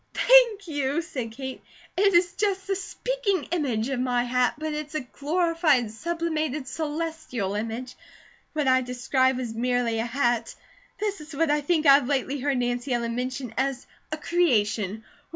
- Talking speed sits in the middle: Yes, average, 165 wpm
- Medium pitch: No, very high, 275 Hz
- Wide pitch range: No, average, 5.0 semitones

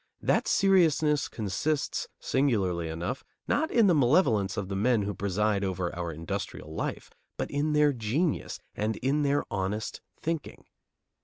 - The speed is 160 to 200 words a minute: No, average, 145 wpm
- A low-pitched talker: Yes, low, 110 Hz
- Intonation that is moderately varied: No, wide, 7.5 semitones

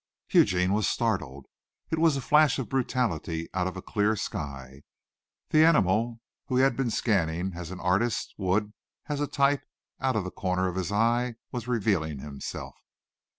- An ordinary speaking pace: Yes, average, 170 wpm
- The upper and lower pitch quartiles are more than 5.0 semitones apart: Yes, wide, 5.6 semitones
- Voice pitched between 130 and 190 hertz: No, low, 105 Hz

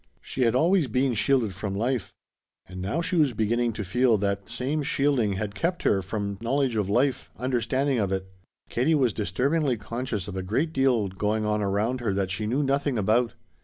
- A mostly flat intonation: No, average, 4.7 semitones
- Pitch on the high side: No, low, 115 Hz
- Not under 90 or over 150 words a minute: No, average, 200 wpm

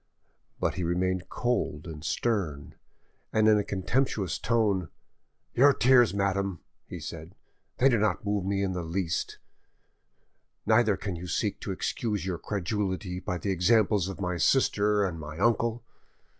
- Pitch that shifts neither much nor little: Yes, average, 3.4 semitones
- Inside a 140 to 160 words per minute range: Yes, average, 150 wpm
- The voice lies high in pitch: No, low, 100 Hz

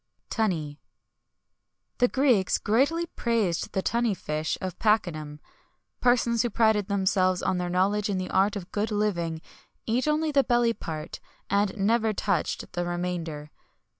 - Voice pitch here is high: Yes, high, 200 Hz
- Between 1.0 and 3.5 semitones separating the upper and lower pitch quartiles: No, average, 4.8 semitones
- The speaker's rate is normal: Yes, average, 160 wpm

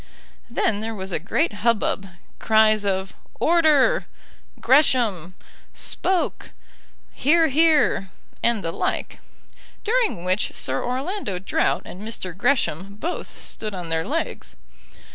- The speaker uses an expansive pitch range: Yes, wide, 7.9 semitones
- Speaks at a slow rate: Yes, slow, 115 wpm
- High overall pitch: Yes, high, 220 Hz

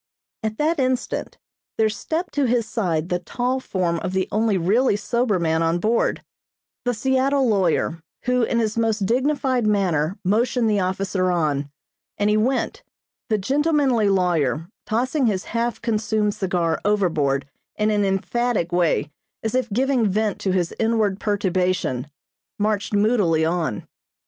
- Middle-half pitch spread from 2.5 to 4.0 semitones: No, average, 4.9 semitones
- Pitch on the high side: Yes, high, 210 Hz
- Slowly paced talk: No, average, 145 wpm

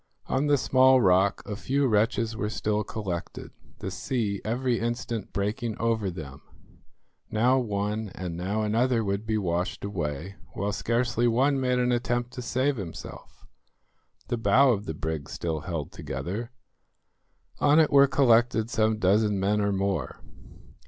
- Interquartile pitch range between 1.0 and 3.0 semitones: No, average, 3.8 semitones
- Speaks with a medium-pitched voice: No, low, 110 Hz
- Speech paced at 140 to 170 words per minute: Yes, average, 150 wpm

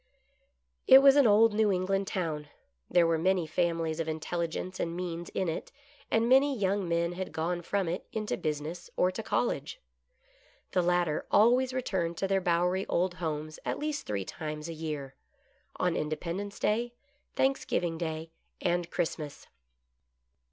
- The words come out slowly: No, average, 155 wpm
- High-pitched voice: No, medium, 175 Hz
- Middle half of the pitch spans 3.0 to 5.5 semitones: Yes, average, 3.7 semitones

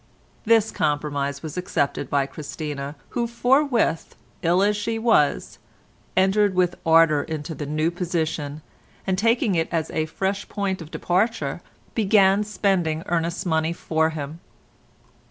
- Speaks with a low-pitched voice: No, medium, 170 Hz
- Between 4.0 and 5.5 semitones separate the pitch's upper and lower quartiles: Yes, average, 4.5 semitones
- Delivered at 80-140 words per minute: Yes, slow, 135 wpm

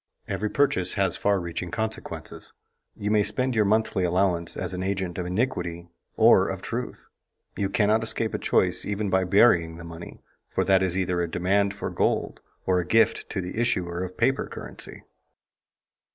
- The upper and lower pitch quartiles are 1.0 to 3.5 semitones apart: Yes, average, 3.1 semitones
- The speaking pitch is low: Yes, very low, 95 Hz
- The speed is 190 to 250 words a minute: No, average, 175 wpm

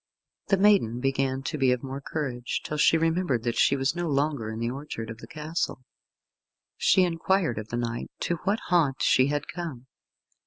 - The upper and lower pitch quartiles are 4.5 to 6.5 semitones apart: Yes, average, 4.9 semitones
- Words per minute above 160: Yes, average, 190 wpm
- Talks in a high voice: No, medium, 140 Hz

